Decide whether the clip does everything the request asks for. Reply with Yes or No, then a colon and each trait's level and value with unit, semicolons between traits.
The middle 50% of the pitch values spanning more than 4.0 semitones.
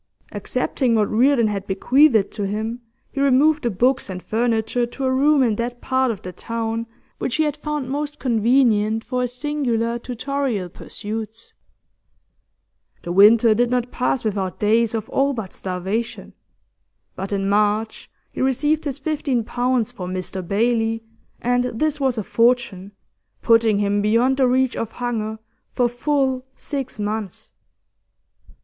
No: average, 3.5 semitones